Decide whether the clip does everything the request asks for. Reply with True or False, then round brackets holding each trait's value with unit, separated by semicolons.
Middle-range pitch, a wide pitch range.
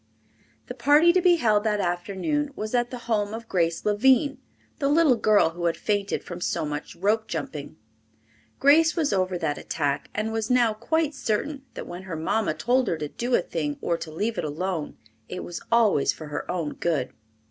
False (210 Hz; 6.6 semitones)